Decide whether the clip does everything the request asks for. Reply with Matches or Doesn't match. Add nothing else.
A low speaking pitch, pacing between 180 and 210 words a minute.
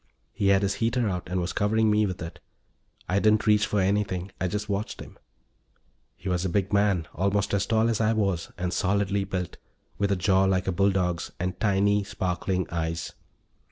Matches